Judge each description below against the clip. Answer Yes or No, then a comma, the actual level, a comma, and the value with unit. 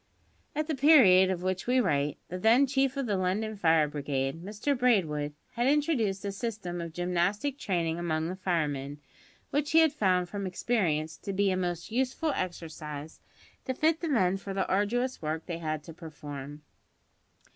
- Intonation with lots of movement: Yes, wide, 7.0 semitones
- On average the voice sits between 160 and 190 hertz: Yes, medium, 185 Hz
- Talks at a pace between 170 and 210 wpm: Yes, average, 175 wpm